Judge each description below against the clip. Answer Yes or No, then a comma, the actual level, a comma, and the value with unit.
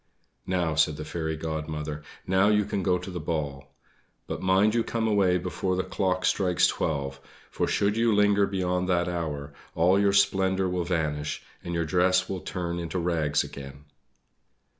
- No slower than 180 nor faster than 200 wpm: No, average, 170 wpm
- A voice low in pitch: Yes, very low, 90 Hz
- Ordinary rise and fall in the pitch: Yes, average, 3.3 semitones